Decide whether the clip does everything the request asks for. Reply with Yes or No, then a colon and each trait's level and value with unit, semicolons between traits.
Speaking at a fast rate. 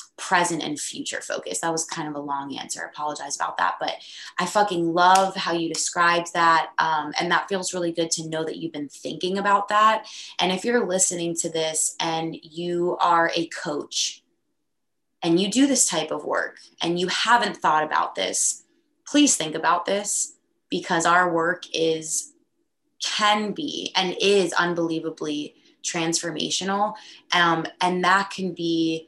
No: average, 165 wpm